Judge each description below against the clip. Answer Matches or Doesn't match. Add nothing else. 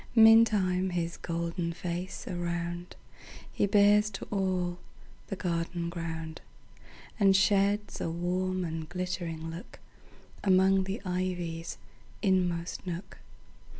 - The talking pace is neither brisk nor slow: Doesn't match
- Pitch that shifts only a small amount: Matches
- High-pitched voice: Doesn't match